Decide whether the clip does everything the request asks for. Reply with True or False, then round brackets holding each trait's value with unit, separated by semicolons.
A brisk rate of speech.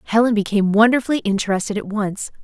False (150 wpm)